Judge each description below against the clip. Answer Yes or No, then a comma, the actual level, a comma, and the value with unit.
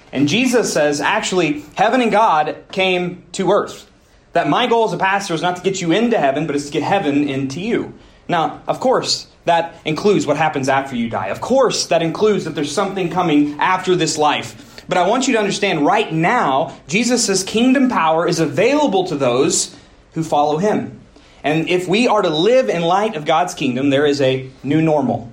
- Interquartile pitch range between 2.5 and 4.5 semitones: No, average, 5.2 semitones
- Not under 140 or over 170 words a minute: No, average, 200 wpm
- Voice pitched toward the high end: No, medium, 170 Hz